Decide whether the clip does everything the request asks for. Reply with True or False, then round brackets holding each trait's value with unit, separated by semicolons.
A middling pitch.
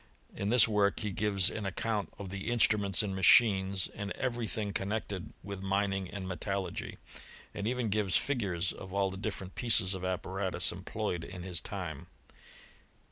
False (100 Hz)